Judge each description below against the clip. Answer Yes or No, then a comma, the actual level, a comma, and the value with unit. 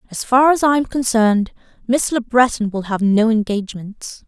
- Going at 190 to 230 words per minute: No, average, 180 wpm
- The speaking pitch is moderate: No, high, 230 Hz